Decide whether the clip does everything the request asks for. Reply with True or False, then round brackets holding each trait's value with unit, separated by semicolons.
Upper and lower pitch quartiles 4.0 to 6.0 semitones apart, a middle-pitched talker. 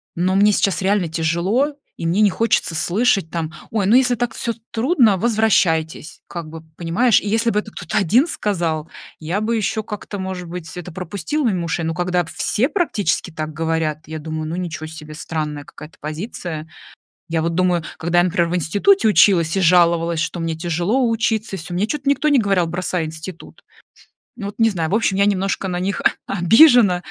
True (4.6 semitones; 180 Hz)